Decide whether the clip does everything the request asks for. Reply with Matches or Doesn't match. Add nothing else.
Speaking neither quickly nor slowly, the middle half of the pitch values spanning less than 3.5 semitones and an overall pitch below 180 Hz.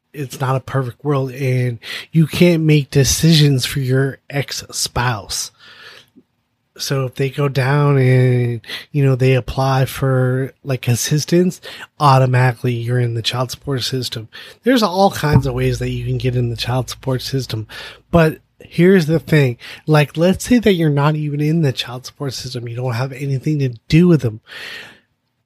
Matches